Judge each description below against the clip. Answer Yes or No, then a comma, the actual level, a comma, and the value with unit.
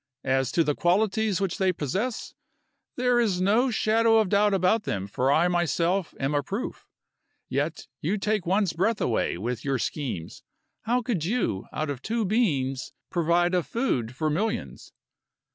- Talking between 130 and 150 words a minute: No, average, 160 wpm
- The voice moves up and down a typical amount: No, wide, 7.0 semitones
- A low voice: No, medium, 180 Hz